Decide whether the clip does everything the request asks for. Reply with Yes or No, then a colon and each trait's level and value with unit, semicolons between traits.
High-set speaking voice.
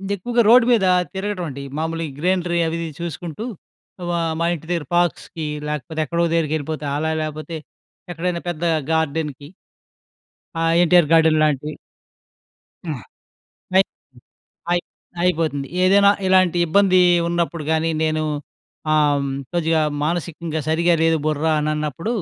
No: medium, 165 Hz